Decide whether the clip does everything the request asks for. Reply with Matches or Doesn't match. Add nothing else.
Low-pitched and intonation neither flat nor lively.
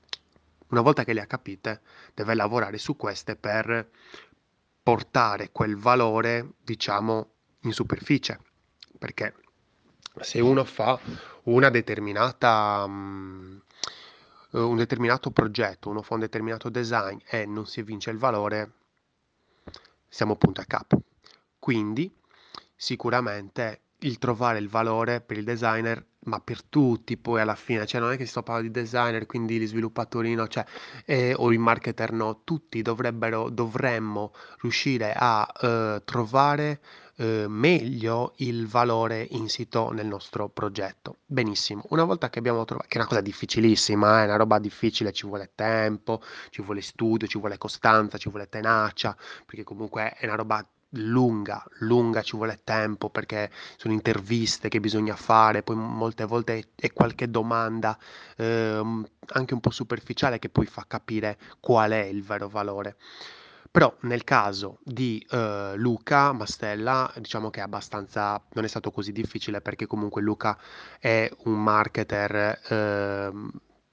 Doesn't match